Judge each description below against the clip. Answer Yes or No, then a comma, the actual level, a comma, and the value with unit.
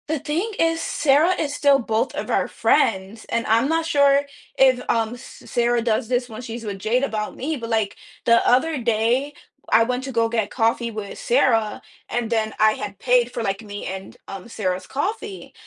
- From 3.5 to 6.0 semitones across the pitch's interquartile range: Yes, average, 4.0 semitones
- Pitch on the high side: Yes, high, 235 Hz